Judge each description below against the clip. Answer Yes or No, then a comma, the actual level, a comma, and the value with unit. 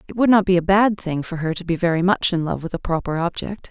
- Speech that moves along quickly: Yes, fast, 310 wpm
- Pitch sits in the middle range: Yes, medium, 180 Hz